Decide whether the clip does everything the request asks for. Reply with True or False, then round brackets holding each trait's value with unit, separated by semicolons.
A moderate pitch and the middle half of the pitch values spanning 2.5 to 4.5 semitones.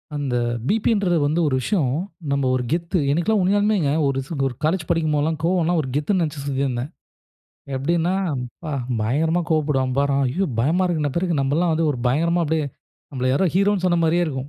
True (160 Hz; 4.0 semitones)